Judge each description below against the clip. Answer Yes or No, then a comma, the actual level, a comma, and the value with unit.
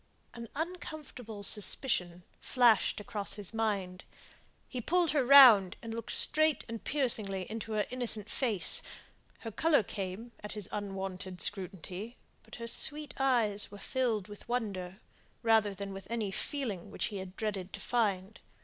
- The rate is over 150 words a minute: No, average, 145 wpm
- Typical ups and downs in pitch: Yes, average, 3.9 semitones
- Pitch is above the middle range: Yes, high, 215 Hz